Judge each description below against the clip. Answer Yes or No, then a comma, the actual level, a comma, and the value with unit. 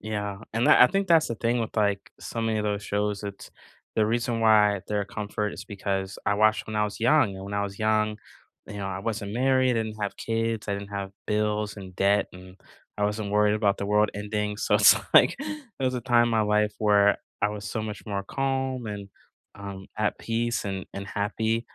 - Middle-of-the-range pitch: No, low, 105 Hz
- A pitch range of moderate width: No, narrow, 1.9 semitones